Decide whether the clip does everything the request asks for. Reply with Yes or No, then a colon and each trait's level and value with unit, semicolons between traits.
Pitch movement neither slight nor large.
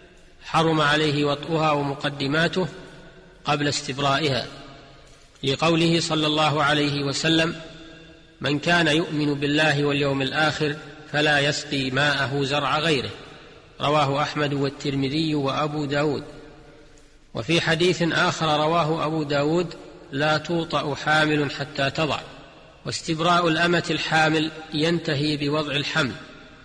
No: narrow, 1.8 semitones